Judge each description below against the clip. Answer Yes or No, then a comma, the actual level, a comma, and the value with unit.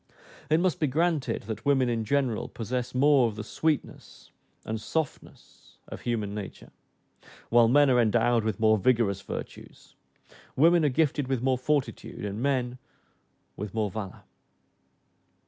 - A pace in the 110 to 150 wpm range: Yes, average, 145 wpm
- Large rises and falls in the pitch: No, average, 4.4 semitones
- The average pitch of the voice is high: No, low, 125 Hz